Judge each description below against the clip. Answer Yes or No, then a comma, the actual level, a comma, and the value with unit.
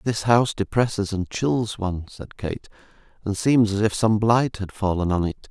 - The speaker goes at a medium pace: Yes, average, 195 wpm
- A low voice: Yes, low, 105 Hz